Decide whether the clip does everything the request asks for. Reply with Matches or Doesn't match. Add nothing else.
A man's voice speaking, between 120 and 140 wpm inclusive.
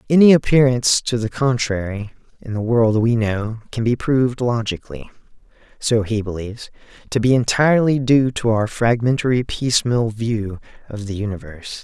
Matches